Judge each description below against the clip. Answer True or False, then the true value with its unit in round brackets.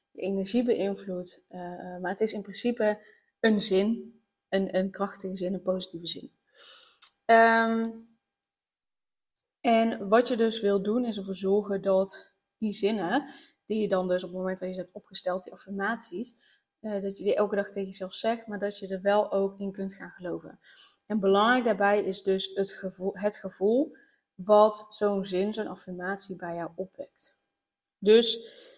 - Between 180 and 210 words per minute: False (170 wpm)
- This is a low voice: False (200 Hz)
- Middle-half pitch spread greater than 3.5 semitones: False (2.7 semitones)